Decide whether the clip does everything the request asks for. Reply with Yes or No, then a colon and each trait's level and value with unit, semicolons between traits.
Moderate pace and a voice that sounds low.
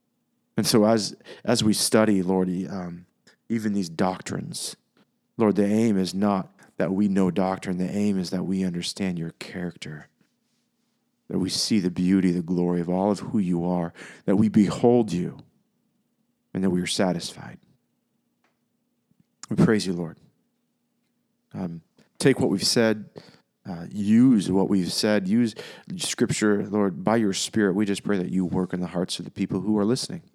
Yes: average, 170 wpm; very low, 95 Hz